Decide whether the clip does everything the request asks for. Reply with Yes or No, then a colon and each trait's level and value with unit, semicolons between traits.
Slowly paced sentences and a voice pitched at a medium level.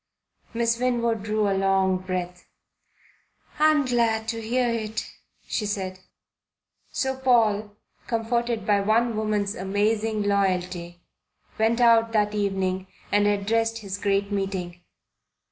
No: slow, 115 wpm; high, 210 Hz